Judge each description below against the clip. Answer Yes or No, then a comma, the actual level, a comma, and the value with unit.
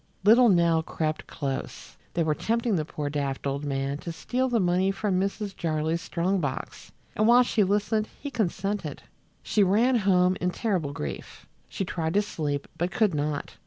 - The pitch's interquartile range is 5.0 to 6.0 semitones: Yes, average, 5.3 semitones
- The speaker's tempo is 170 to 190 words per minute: Yes, average, 175 wpm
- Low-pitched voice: No, medium, 180 Hz